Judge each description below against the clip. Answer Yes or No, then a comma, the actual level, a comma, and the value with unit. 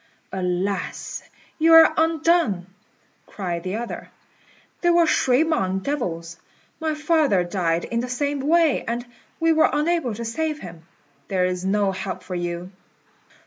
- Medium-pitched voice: No, high, 230 Hz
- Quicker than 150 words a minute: No, average, 145 wpm